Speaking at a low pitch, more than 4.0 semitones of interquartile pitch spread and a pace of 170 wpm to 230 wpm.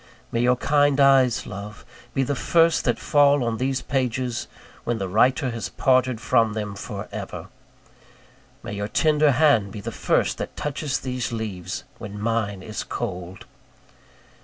No: low, 120 Hz; average, 4.4 semitones; average, 155 wpm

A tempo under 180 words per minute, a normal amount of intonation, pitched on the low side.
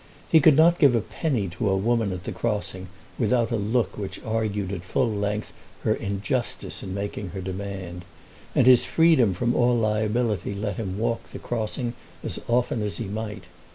No: average, 185 wpm; average, 3.2 semitones; low, 105 Hz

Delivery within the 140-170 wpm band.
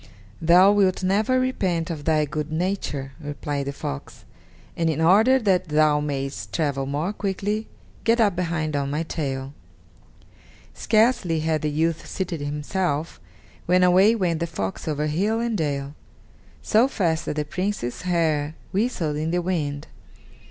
Yes: average, 150 wpm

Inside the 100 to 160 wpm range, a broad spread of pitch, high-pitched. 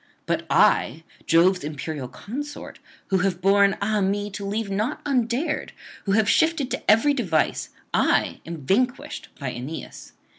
Yes: average, 145 wpm; wide, 6.3 semitones; high, 200 Hz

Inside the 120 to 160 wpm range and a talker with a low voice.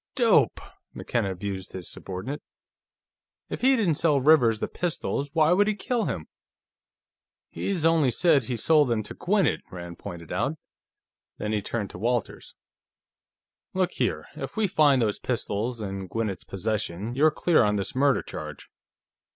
Yes: average, 150 wpm; low, 125 Hz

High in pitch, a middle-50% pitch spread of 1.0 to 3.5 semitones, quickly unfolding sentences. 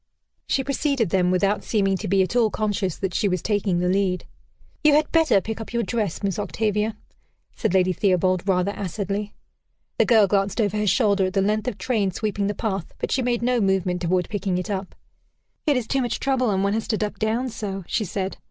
Yes: high, 205 Hz; average, 2.8 semitones; fast, 215 wpm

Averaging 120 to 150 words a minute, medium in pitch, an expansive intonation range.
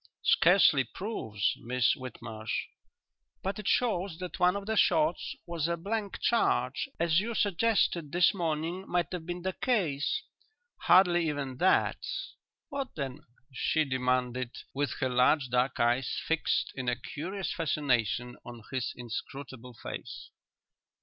Yes: slow, 135 wpm; medium, 155 Hz; wide, 6.5 semitones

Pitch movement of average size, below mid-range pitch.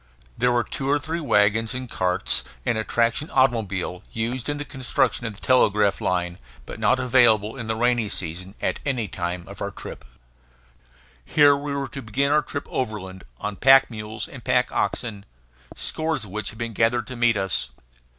Yes: average, 4.1 semitones; low, 115 Hz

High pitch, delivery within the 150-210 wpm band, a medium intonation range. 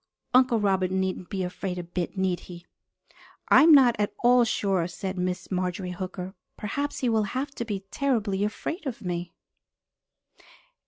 Yes: high, 195 Hz; average, 160 wpm; average, 4.6 semitones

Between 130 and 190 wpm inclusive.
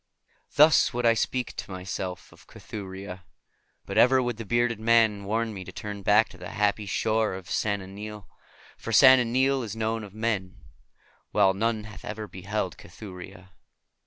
Yes: average, 165 wpm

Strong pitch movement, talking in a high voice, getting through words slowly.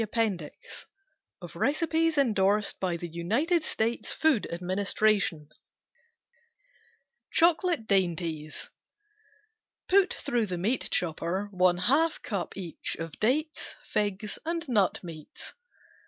Yes: wide, 8.0 semitones; high, 205 Hz; slow, 95 wpm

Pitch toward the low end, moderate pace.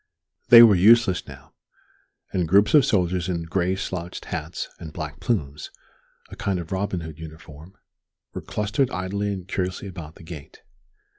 Yes: very low, 90 Hz; average, 155 wpm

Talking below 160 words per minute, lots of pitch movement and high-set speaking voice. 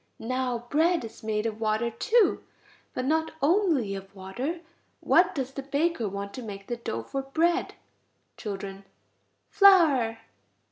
Yes: average, 140 wpm; wide, 7.1 semitones; very high, 250 Hz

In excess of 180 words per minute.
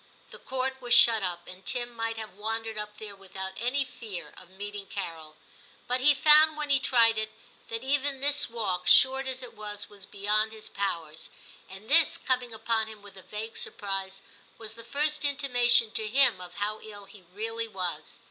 Yes: average, 190 wpm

